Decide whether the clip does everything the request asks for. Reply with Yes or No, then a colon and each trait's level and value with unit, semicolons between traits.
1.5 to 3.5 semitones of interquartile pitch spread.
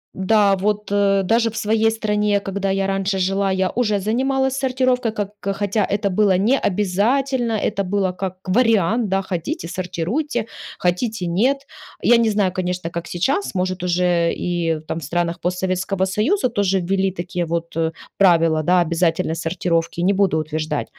Yes: average, 3.2 semitones